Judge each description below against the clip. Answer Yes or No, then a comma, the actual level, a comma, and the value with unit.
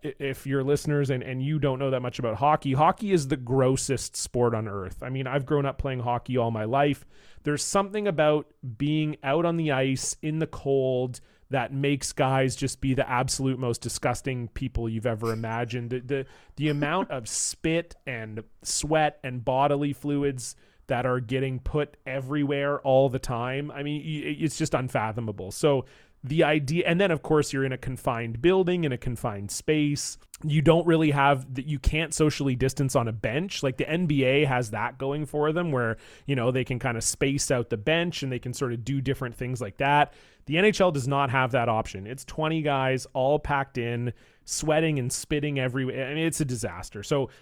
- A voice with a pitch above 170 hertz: No, low, 135 Hz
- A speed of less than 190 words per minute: No, average, 200 wpm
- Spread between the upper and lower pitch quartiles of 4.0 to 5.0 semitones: No, average, 2.9 semitones